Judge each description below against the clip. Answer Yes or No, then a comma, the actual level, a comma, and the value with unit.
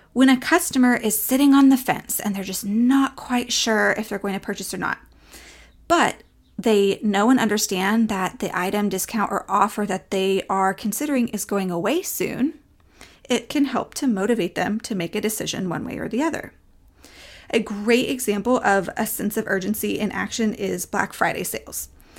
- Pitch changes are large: No, average, 3.8 semitones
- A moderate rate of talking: Yes, average, 185 wpm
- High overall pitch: Yes, high, 215 Hz